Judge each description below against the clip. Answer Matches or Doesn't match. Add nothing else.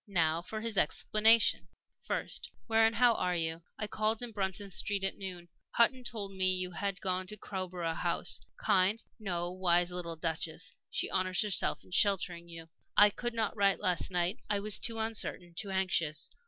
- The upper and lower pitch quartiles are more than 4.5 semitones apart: Doesn't match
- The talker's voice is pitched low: Doesn't match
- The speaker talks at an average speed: Matches